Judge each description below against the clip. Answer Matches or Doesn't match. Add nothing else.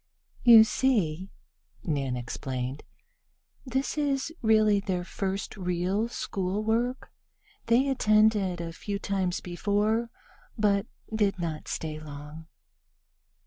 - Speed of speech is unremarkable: Doesn't match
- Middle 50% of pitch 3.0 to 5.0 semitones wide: Matches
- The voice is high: Matches